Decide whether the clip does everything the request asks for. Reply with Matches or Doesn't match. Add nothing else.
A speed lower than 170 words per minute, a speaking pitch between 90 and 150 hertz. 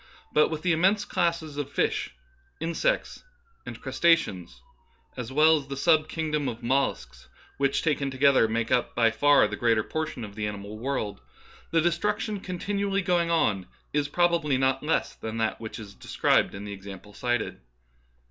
Doesn't match